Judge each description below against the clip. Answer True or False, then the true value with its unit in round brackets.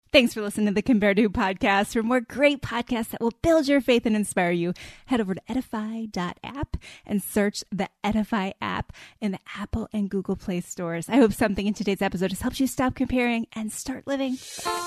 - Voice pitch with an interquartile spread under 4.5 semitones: True (3.9 semitones)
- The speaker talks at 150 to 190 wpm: False (200 wpm)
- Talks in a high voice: True (215 Hz)